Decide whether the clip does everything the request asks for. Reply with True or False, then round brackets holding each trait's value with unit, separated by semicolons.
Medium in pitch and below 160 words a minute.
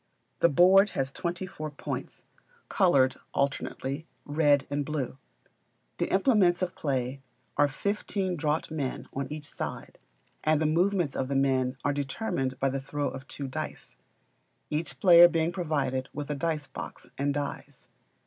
True (145 Hz; 150 wpm)